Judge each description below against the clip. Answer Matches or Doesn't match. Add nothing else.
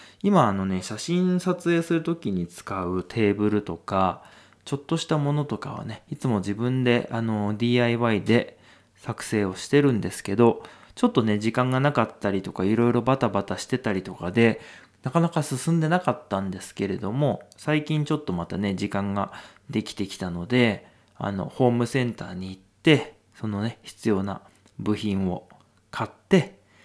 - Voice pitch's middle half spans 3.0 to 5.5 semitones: Doesn't match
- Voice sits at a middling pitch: Doesn't match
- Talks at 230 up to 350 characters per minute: Matches